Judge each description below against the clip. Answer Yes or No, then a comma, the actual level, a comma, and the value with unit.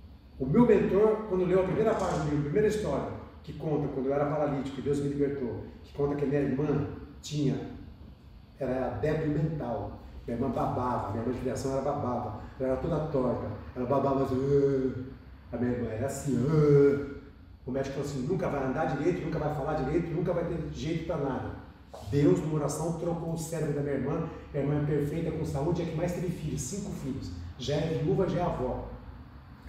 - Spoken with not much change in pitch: No, average, 3.8 semitones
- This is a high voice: No, medium, 140 Hz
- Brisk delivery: Yes, fast, 200 wpm